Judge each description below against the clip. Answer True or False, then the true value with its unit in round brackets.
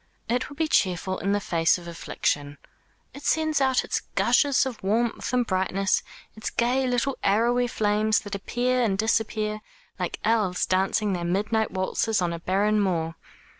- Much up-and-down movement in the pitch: False (4.3 semitones)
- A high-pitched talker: True (210 Hz)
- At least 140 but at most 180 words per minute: True (165 wpm)